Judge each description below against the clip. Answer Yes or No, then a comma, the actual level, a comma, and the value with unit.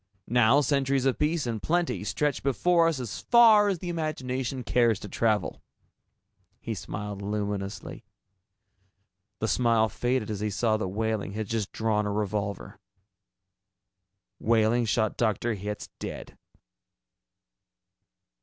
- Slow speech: Yes, slow, 125 wpm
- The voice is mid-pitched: No, low, 115 Hz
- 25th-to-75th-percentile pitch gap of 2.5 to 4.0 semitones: No, average, 4.4 semitones